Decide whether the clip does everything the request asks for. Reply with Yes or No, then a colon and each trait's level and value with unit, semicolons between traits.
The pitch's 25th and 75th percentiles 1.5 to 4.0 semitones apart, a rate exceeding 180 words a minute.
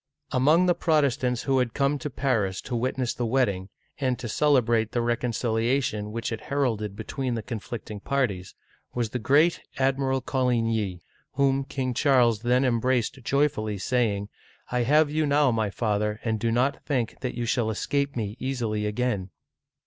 No: average, 3.4 semitones; average, 170 wpm